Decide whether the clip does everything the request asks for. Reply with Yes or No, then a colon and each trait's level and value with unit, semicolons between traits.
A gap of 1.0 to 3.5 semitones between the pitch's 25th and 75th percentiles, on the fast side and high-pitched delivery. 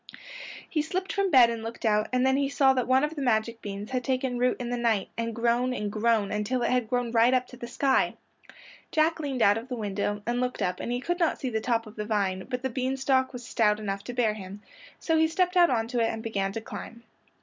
Yes: average, 3.2 semitones; fast, 260 wpm; high, 240 Hz